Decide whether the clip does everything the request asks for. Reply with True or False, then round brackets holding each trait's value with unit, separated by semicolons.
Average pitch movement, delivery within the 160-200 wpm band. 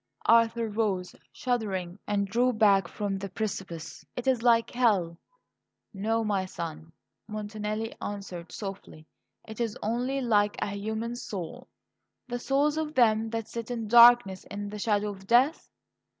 False (3.1 semitones; 150 wpm)